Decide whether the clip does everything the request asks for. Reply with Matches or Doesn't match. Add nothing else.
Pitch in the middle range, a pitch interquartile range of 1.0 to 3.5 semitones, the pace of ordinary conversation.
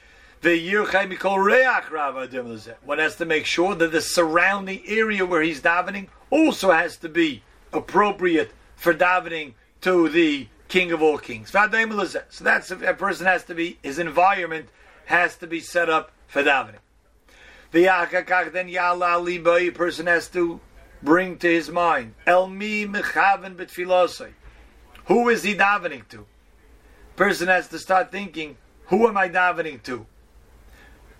Doesn't match